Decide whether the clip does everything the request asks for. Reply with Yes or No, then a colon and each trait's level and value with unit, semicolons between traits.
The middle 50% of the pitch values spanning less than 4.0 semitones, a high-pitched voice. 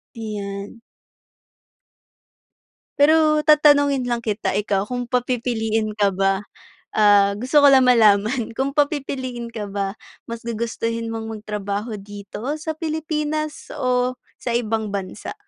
No: average, 4.7 semitones; high, 230 Hz